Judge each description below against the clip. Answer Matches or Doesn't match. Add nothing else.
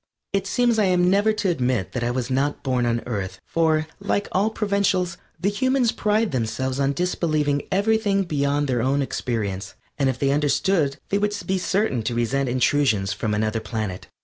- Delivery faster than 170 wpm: Matches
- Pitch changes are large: Matches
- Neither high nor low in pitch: Matches